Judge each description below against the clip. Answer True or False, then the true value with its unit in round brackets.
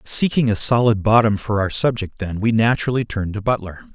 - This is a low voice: True (110 Hz)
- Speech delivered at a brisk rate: True (215 wpm)